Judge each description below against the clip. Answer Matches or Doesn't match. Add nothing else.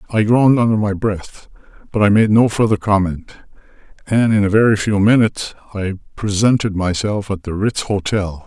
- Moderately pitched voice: Doesn't match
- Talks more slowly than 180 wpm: Matches